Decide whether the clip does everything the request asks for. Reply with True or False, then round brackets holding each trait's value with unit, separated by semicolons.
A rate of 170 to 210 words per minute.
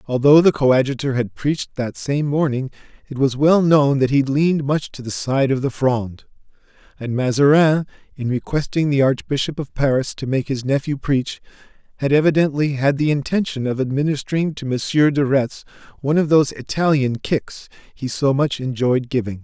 True (175 wpm)